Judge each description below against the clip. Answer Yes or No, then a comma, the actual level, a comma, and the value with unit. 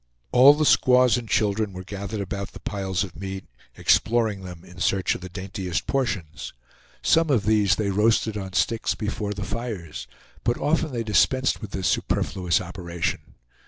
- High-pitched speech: No, low, 100 Hz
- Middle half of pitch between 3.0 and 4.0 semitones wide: Yes, average, 3.6 semitones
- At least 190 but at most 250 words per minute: No, average, 165 wpm